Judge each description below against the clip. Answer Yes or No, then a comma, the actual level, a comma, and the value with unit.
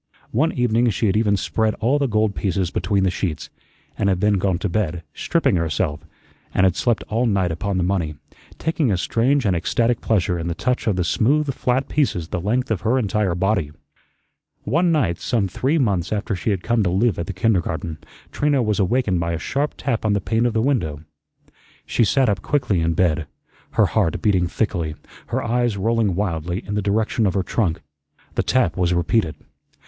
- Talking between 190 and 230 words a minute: Yes, average, 200 wpm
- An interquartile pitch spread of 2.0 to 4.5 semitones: No, average, 4.9 semitones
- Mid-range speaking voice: No, low, 100 Hz